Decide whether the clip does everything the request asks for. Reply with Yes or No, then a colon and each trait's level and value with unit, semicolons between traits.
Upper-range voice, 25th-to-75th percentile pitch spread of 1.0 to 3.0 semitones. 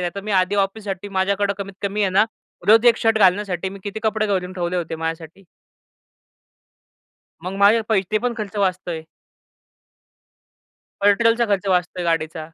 Yes: high, 195 Hz; average, 2.7 semitones